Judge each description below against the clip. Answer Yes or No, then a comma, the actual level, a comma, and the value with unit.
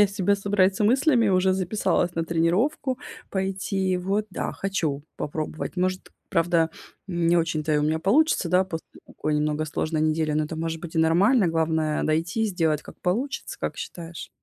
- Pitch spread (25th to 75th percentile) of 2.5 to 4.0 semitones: Yes, average, 3.5 semitones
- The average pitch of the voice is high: No, medium, 175 Hz